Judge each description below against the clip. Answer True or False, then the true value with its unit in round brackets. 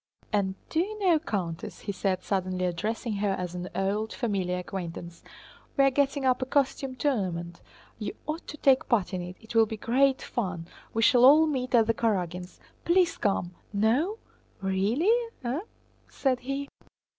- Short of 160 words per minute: False (170 wpm)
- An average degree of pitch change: False (6.5 semitones)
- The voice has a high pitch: True (220 Hz)